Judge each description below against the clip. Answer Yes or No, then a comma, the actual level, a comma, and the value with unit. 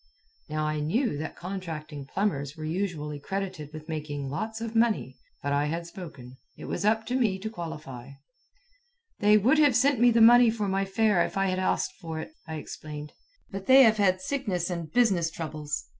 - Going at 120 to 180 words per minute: No, average, 190 wpm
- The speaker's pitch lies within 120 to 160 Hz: No, medium, 180 Hz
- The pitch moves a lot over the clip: Yes, wide, 6.1 semitones